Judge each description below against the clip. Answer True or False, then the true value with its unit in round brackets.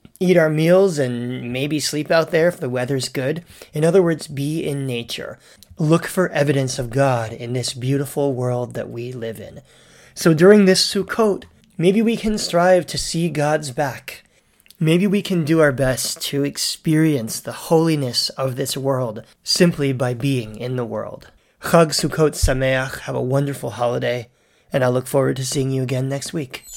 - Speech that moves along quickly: False (175 wpm)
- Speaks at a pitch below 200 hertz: True (140 Hz)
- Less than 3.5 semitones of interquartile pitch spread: False (4.7 semitones)